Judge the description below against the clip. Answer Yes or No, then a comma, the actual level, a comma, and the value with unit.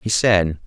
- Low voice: Yes, low, 100 Hz